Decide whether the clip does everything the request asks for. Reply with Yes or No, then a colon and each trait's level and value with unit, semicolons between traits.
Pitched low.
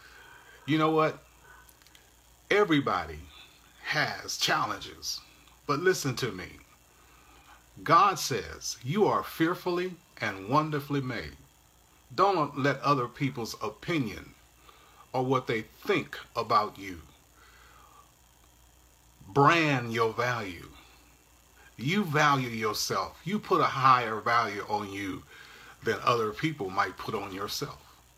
Yes: low, 115 Hz